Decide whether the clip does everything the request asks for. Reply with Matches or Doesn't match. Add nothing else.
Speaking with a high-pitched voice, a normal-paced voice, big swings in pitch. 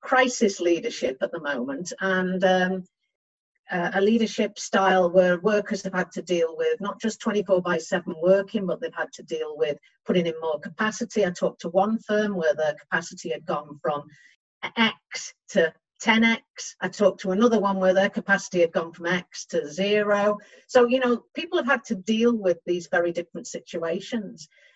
Doesn't match